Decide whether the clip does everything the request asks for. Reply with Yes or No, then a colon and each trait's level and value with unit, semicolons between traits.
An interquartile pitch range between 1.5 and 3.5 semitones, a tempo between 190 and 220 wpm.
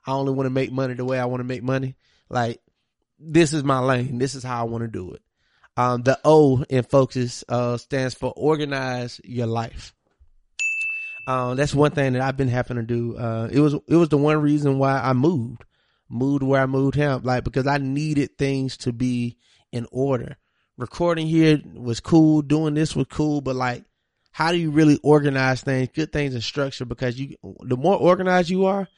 Yes: average, 3.1 semitones; fast, 205 wpm